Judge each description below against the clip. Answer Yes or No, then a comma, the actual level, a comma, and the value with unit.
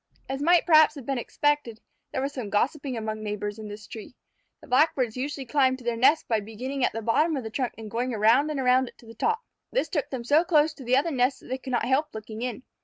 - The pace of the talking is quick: Yes, fast, 255 wpm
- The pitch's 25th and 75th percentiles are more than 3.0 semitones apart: Yes, average, 4.3 semitones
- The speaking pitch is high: Yes, very high, 255 Hz